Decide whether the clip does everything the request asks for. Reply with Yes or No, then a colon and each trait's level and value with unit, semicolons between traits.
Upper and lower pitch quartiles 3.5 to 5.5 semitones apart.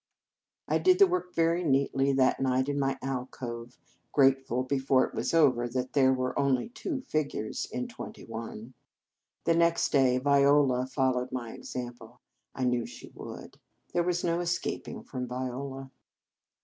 No: average, 3.1 semitones